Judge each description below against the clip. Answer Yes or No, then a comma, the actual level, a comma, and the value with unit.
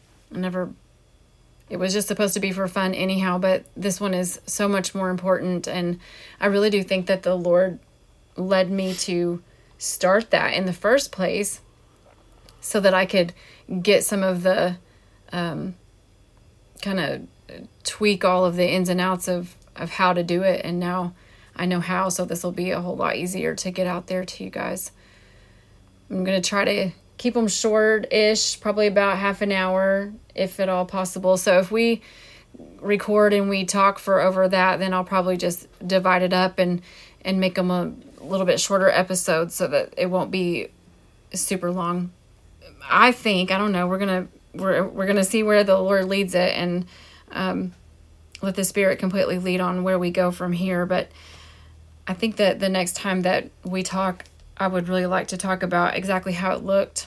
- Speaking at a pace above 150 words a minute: Yes, average, 190 wpm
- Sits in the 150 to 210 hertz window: Yes, medium, 185 Hz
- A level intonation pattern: Yes, narrow, 1.5 semitones